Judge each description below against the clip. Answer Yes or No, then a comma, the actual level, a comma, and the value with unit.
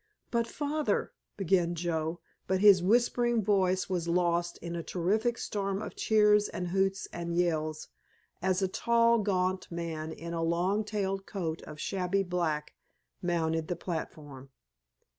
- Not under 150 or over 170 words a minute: No, average, 140 wpm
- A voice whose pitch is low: No, medium, 180 Hz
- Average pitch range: Yes, average, 3.1 semitones